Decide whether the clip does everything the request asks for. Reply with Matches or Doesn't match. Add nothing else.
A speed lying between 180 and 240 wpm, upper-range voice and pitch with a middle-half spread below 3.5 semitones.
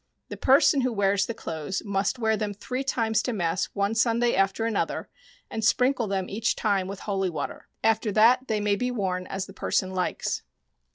Matches